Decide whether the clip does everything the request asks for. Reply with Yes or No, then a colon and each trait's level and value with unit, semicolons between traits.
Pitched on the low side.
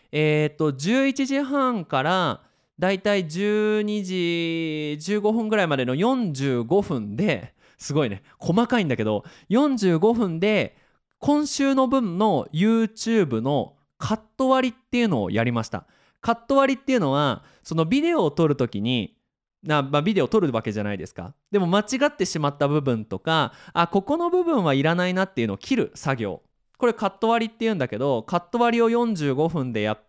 No: high, 190 Hz